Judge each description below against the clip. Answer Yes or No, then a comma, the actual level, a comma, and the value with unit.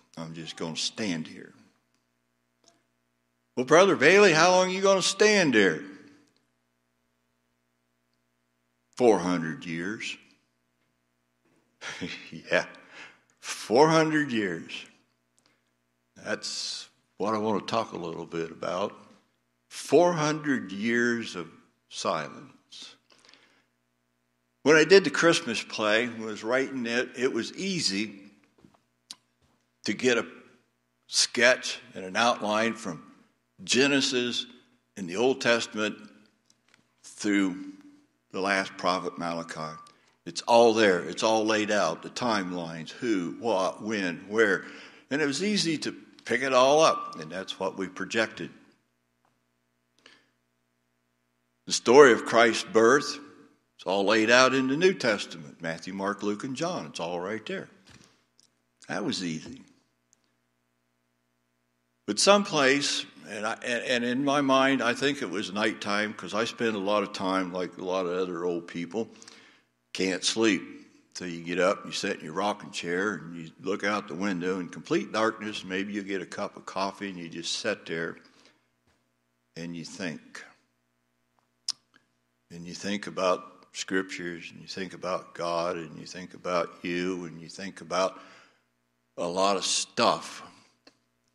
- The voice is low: Yes, very low, 85 Hz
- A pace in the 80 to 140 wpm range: Yes, slow, 135 wpm